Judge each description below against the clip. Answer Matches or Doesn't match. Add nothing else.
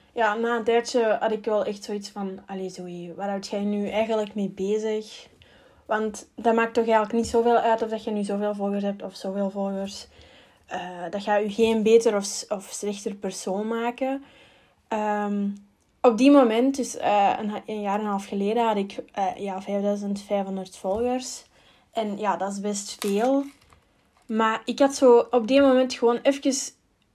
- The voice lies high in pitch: Matches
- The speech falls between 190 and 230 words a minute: Doesn't match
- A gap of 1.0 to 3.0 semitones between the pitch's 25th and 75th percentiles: Matches